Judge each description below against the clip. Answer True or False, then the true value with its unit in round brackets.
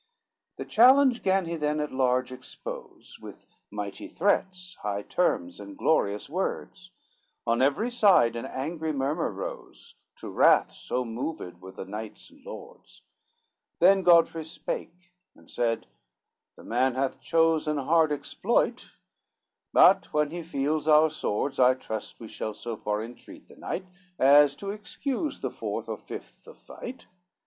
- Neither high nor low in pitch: True (150 Hz)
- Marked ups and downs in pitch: True (6.4 semitones)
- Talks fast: False (150 wpm)